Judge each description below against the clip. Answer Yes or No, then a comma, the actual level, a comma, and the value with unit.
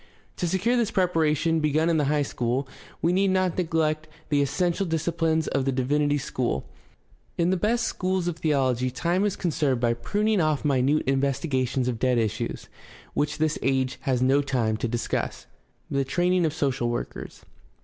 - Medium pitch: Yes, medium, 150 Hz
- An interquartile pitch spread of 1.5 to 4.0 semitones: No, average, 4.7 semitones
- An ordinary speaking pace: Yes, average, 170 wpm